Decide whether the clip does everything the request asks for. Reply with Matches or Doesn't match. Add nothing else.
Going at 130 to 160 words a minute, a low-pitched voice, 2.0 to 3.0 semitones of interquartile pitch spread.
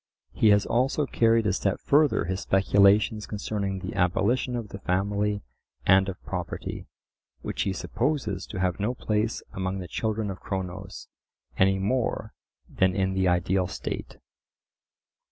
Matches